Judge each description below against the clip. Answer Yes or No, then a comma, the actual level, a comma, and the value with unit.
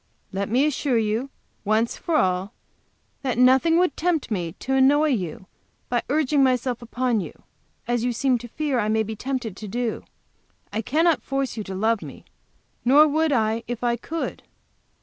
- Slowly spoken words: No, average, 175 wpm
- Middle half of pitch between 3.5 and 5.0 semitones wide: Yes, average, 4.0 semitones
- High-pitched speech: Yes, high, 245 Hz